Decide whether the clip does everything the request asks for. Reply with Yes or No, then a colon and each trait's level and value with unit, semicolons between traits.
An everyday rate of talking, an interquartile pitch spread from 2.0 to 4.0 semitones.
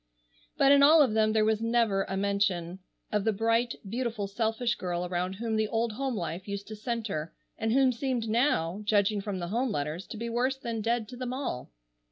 No: fast, 210 wpm; average, 3.3 semitones